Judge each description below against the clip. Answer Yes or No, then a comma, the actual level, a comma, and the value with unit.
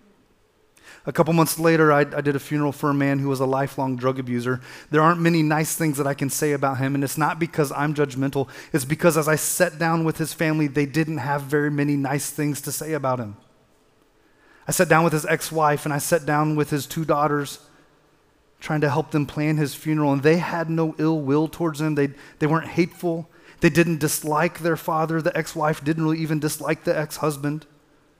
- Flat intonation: Yes, narrow, 1.8 semitones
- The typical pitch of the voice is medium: Yes, medium, 150 Hz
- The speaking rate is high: Yes, fast, 220 wpm